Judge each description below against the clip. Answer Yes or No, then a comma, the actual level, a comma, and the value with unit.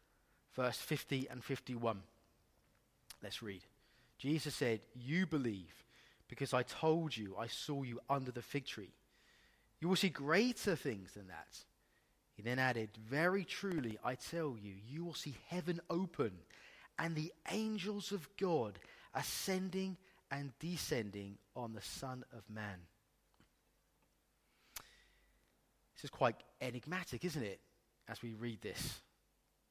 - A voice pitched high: No, low, 135 Hz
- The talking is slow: Yes, slow, 130 wpm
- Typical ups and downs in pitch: No, wide, 6.6 semitones